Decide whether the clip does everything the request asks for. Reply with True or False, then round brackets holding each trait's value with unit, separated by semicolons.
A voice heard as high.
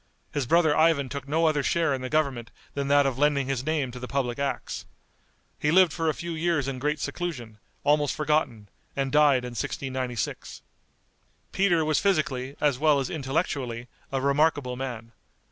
False (140 Hz)